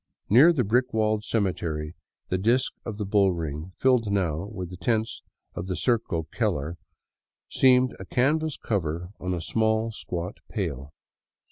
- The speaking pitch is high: No, low, 100 Hz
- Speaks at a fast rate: No, average, 150 wpm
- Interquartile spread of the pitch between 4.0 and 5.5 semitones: Yes, average, 4.8 semitones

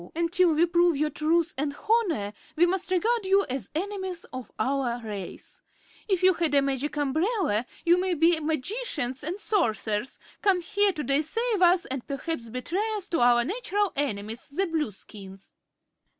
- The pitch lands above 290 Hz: Yes, very high, 325 Hz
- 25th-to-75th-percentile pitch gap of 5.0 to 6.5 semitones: Yes, wide, 6.1 semitones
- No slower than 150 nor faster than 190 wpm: Yes, average, 160 wpm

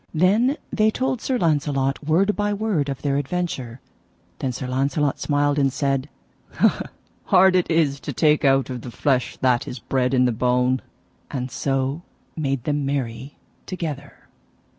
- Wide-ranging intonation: No, average, 3.9 semitones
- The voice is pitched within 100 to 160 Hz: Yes, medium, 140 Hz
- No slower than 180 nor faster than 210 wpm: No, average, 155 wpm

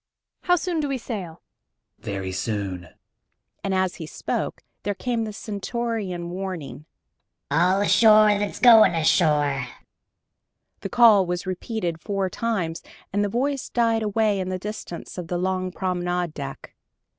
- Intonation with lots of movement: No, average, 4.2 semitones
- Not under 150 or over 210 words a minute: No, average, 140 wpm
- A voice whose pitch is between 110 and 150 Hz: No, high, 190 Hz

